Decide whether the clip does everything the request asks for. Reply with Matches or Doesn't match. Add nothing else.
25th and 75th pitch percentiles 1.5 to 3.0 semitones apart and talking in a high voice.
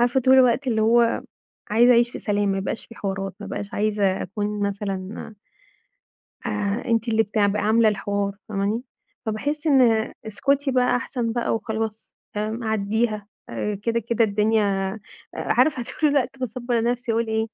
Matches